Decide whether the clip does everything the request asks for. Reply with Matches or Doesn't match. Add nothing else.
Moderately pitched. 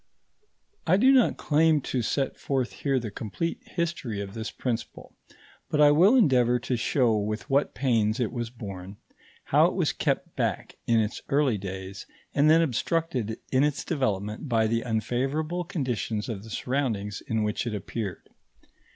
Doesn't match